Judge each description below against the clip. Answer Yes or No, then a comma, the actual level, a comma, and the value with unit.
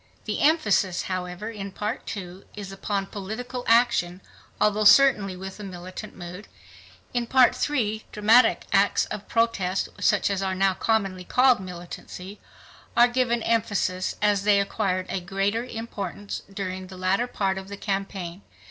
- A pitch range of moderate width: Yes, average, 3.3 semitones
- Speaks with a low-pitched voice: No, high, 200 Hz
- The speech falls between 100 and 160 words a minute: Yes, average, 150 wpm